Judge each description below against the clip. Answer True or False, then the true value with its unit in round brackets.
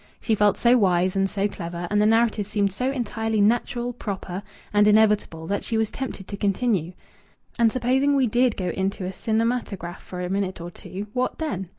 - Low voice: False (210 Hz)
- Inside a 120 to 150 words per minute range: False (195 wpm)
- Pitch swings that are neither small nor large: True (3.8 semitones)